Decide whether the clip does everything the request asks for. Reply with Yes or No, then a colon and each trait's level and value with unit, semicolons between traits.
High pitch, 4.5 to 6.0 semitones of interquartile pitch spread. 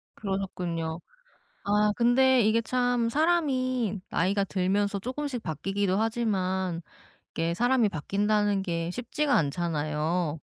Yes: high, 200 Hz; average, 5.3 semitones